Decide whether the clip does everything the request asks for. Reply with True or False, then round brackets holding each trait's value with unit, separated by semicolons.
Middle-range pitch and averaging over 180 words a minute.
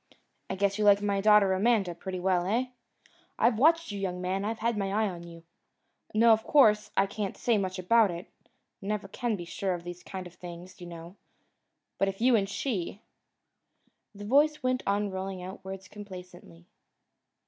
False (195 Hz; 190 wpm)